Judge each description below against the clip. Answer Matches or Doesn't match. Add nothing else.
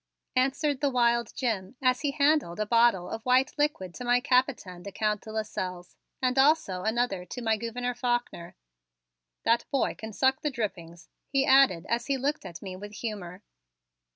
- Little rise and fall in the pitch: Doesn't match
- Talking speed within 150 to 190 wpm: Matches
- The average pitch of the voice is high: Matches